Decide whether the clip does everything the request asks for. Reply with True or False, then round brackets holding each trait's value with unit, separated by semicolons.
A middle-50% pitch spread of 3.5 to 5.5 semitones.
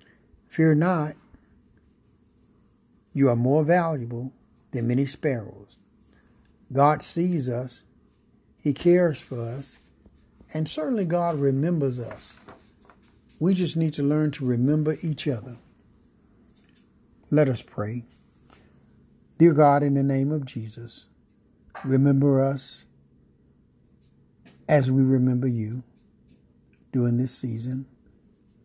True (3.9 semitones)